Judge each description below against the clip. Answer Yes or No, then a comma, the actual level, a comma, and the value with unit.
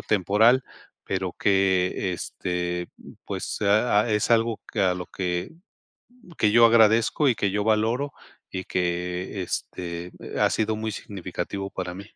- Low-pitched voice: Yes, low, 100 Hz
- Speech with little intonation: No, average, 3.4 semitones